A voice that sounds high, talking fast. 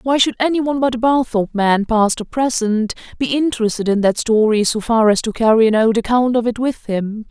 Yes: high, 230 Hz; fast, 230 wpm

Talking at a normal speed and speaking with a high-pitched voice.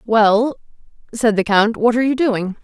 Yes: average, 180 wpm; high, 225 Hz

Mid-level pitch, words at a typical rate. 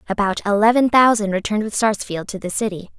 No: high, 210 Hz; average, 180 wpm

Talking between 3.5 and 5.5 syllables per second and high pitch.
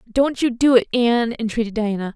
No: 5.7 syllables/s; high, 235 Hz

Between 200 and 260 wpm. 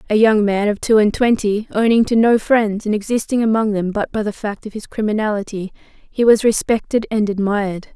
Yes: fast, 205 wpm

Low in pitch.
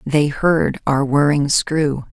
No: medium, 145 Hz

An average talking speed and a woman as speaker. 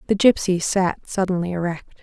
Yes: average, 150 wpm; female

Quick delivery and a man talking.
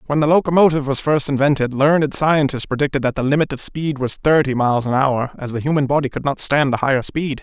Yes: fast, 235 wpm; male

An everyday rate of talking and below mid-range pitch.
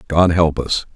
Yes: average, 190 wpm; very low, 80 Hz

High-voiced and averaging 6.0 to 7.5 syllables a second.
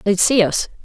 No: high, 205 Hz; 5.0 syllables/s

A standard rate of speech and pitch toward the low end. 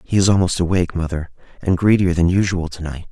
No: fast, 210 wpm; very low, 90 Hz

